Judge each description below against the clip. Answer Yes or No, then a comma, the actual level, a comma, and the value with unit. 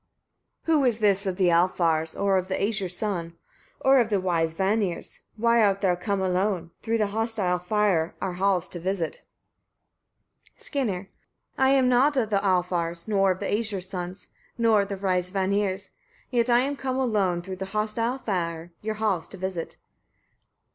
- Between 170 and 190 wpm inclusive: Yes, average, 175 wpm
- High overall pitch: Yes, high, 195 Hz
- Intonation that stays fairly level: No, average, 3.4 semitones